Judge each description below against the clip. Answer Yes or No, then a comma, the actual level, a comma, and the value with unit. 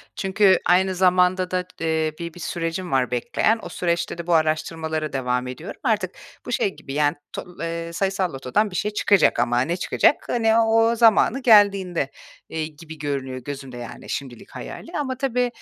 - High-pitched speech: No, medium, 170 Hz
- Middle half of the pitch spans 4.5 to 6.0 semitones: Yes, average, 5.2 semitones